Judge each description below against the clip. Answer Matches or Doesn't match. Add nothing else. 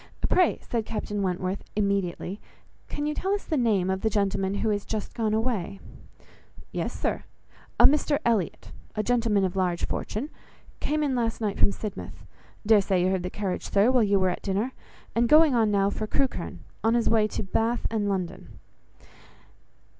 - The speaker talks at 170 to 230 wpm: Matches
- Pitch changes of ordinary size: Matches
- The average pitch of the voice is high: Matches